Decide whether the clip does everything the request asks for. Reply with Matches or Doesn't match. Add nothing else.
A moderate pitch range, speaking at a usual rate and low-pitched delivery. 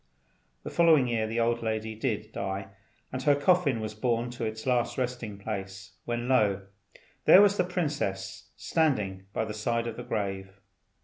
Matches